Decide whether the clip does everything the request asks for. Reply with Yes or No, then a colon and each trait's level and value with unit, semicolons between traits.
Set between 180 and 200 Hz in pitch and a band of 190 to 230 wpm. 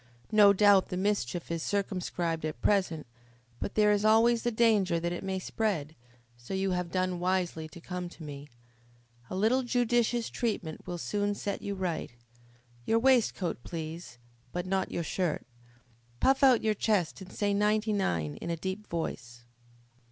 No: high, 190 Hz; average, 165 wpm